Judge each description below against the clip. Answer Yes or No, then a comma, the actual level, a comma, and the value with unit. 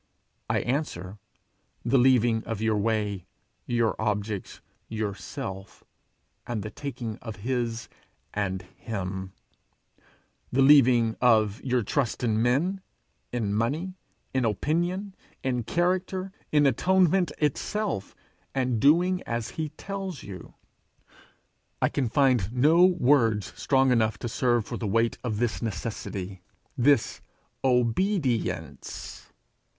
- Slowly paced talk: Yes, slow, 115 wpm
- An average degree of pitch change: Yes, average, 5.0 semitones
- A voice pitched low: Yes, low, 120 Hz